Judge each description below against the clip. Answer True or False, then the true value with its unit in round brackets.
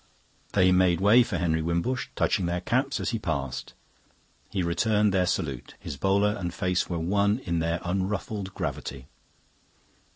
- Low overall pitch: True (90 Hz)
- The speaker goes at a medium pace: True (155 wpm)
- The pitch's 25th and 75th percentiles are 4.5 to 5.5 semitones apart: False (3.3 semitones)